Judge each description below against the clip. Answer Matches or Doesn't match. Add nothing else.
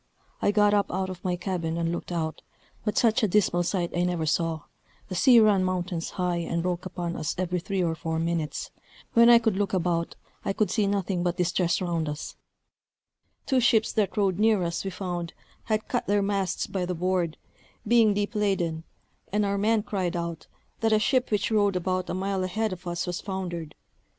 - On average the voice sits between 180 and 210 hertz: Matches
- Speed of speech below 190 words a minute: Doesn't match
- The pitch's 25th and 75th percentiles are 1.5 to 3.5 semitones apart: Matches